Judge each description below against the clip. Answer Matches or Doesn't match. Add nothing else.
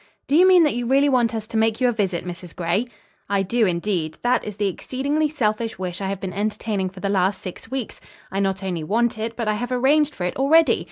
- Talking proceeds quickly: Matches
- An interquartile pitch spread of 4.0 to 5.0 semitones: Matches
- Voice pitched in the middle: Doesn't match